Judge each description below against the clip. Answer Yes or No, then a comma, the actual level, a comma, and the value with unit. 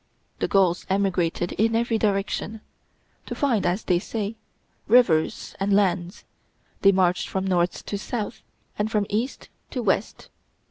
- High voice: Yes, high, 200 Hz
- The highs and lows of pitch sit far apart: No, average, 3.1 semitones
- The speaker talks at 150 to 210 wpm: No, average, 140 wpm